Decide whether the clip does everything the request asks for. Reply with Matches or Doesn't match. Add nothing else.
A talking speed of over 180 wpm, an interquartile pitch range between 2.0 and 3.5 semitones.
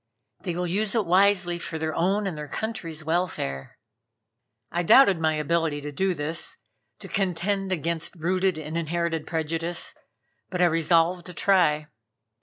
Doesn't match